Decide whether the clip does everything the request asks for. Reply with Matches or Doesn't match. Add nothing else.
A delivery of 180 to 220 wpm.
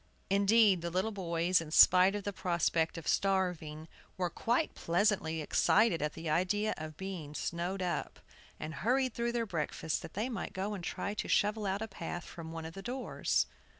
Matches